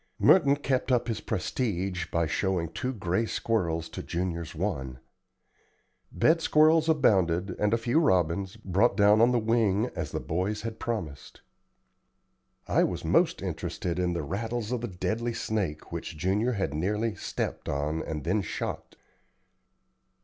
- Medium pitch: No, low, 100 Hz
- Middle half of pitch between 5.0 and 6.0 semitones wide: Yes, wide, 5.4 semitones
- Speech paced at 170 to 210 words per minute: No, average, 150 wpm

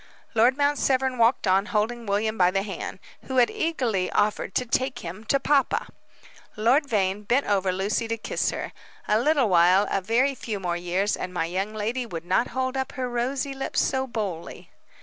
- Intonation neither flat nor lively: Yes, average, 5.0 semitones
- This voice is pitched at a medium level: No, high, 225 Hz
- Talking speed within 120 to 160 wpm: No, average, 190 wpm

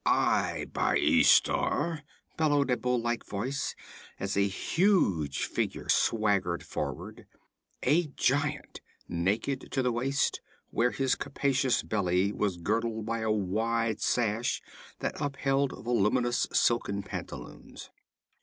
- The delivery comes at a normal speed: No, slow, 115 wpm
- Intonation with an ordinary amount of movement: Yes, average, 5.0 semitones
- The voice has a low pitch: Yes, low, 115 Hz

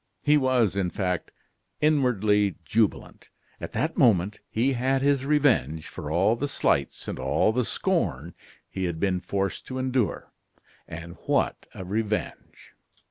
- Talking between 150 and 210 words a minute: No, average, 140 wpm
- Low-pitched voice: Yes, low, 110 Hz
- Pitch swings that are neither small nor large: No, wide, 5.7 semitones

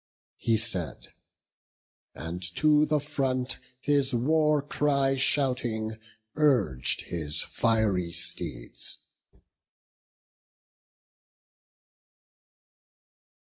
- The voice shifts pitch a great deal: Yes, wide, 6.2 semitones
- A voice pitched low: Yes, low, 130 Hz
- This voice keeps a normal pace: No, slow, 60 wpm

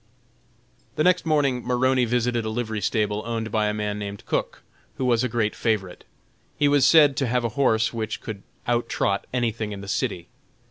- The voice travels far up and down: No, average, 3.0 semitones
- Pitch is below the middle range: Yes, low, 115 Hz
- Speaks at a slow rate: No, average, 190 wpm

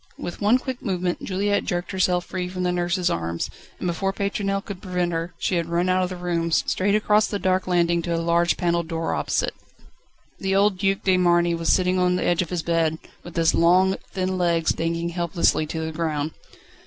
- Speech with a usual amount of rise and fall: No, narrow, 1.8 semitones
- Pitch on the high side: No, medium, 180 Hz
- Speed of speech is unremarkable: No, fast, 210 wpm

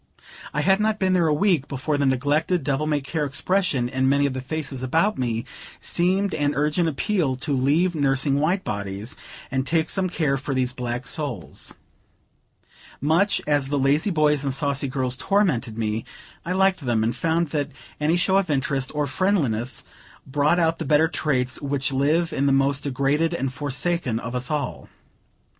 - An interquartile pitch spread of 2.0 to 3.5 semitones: No, average, 3.9 semitones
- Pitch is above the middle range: No, medium, 145 Hz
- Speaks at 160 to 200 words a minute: Yes, average, 180 wpm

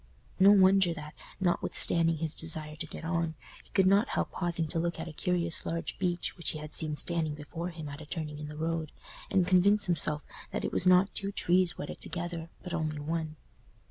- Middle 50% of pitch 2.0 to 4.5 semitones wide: Yes, narrow, 2.5 semitones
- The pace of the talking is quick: Yes, fast, 210 wpm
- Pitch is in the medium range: Yes, medium, 165 Hz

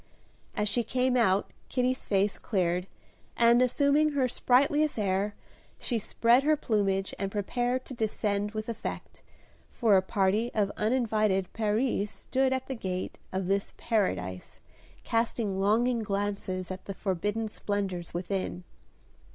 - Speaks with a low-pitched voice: No, high, 210 Hz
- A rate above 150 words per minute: No, slow, 135 wpm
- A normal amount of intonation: Yes, average, 4.0 semitones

